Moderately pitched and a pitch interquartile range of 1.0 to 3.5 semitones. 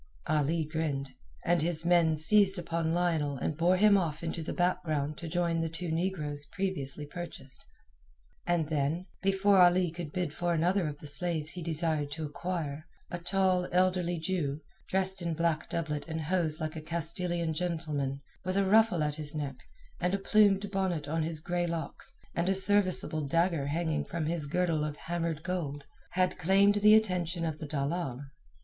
Yes: medium, 170 Hz; average, 2.8 semitones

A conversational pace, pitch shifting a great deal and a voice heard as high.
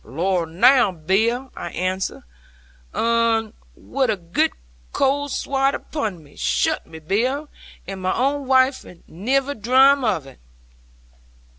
No: slow, 125 wpm; wide, 6.6 semitones; high, 225 Hz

